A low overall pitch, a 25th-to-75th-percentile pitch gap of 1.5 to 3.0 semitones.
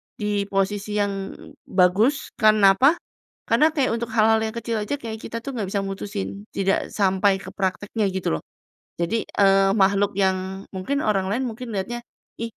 No: high, 205 Hz; narrow, 2.6 semitones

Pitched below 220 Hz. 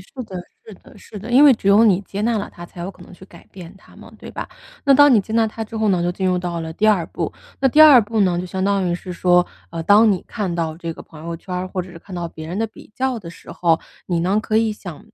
Yes: high, 190 Hz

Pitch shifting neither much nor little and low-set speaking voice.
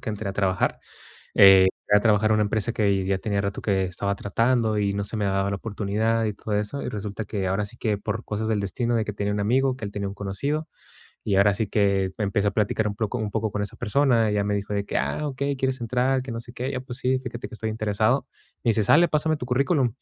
Yes: average, 3.1 semitones; low, 105 Hz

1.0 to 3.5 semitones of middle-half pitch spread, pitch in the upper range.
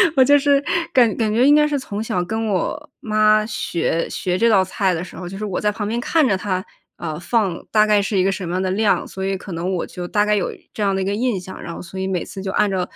Yes: average, 3.0 semitones; high, 200 Hz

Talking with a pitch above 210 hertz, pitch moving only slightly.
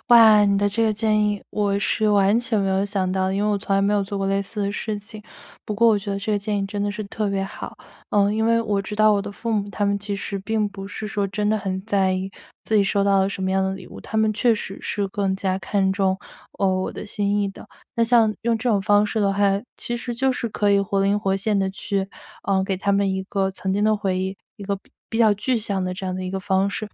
No: high, 200 Hz; narrow, 1.5 semitones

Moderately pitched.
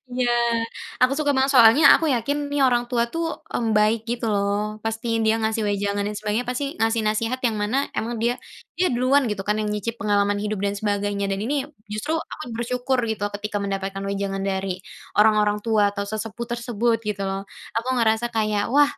No: high, 220 Hz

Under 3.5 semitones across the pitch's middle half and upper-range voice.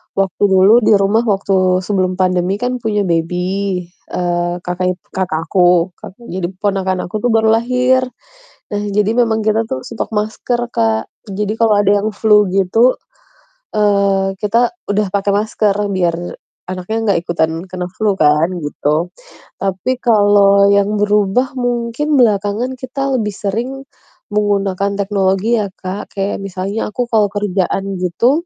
Yes: average, 2.8 semitones; high, 200 Hz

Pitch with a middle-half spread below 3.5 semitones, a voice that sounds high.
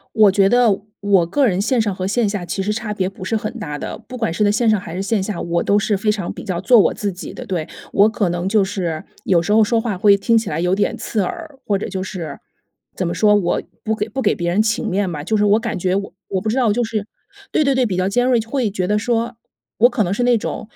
Yes: average, 3.1 semitones; high, 205 Hz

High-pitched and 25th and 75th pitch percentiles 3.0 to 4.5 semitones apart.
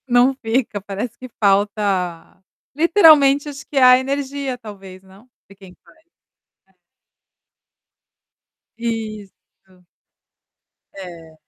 No: high, 220 Hz; wide, 5.4 semitones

